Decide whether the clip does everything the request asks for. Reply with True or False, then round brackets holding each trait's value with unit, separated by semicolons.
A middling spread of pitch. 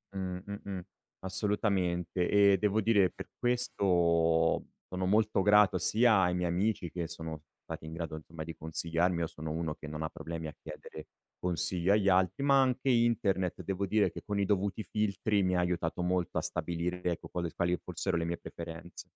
True (3.3 semitones)